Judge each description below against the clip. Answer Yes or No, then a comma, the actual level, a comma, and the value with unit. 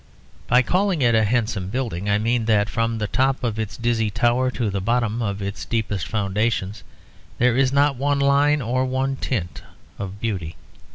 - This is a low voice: Yes, low, 115 Hz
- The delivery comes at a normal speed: Yes, average, 180 wpm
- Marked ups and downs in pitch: No, average, 3.8 semitones